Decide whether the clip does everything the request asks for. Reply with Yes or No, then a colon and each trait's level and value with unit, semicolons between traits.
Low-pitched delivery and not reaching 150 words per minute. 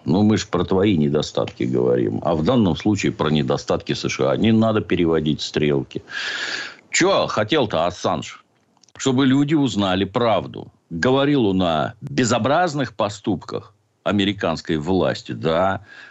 Yes: low, 100 Hz; average, 125 wpm